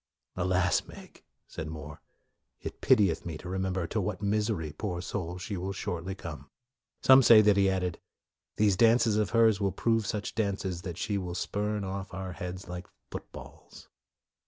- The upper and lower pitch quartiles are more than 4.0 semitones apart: No, average, 2.9 semitones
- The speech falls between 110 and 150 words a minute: No, average, 180 wpm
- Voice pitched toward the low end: Yes, very low, 95 Hz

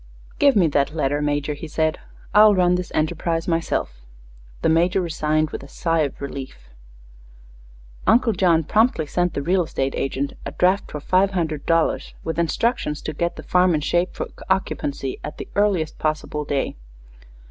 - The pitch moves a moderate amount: Yes, average, 3.4 semitones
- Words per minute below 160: No, average, 170 wpm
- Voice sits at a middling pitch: Yes, medium, 165 Hz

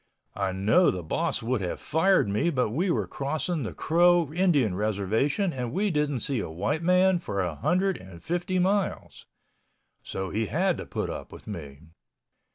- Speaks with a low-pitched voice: No, medium, 145 Hz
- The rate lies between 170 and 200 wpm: Yes, average, 175 wpm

